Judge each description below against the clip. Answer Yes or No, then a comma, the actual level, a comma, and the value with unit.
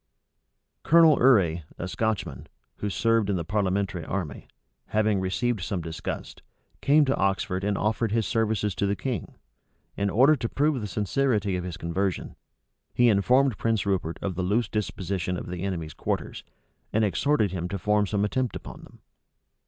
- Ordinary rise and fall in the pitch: Yes, average, 3.7 semitones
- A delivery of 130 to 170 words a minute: Yes, average, 165 wpm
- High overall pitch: No, low, 100 Hz